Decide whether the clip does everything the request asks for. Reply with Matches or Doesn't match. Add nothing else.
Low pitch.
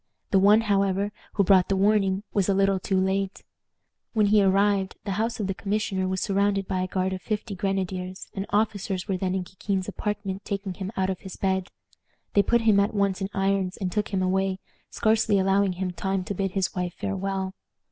Doesn't match